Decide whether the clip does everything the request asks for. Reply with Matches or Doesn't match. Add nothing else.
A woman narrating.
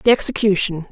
Matches